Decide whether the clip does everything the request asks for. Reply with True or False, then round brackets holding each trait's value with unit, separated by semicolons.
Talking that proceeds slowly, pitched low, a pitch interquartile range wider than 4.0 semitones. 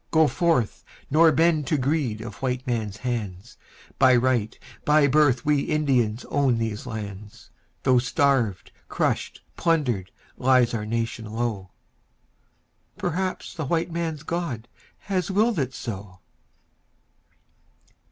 True (120 wpm; 130 Hz; 5.4 semitones)